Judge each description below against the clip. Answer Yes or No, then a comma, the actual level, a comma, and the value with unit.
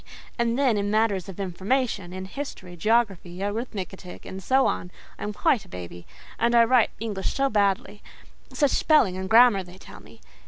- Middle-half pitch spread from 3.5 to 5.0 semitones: Yes, average, 4.0 semitones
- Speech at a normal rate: Yes, average, 165 wpm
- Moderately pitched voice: No, high, 205 Hz